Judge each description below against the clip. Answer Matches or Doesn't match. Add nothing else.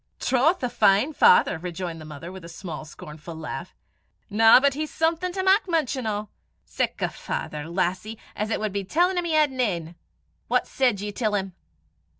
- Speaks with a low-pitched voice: Doesn't match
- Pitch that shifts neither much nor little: Doesn't match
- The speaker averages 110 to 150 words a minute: Doesn't match